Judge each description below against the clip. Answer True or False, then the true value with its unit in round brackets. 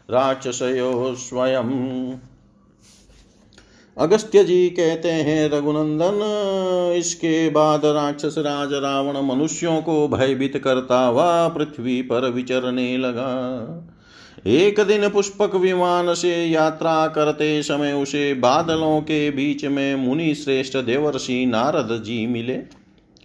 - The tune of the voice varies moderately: True (3.9 semitones)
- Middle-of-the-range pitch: True (145 Hz)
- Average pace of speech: False (105 wpm)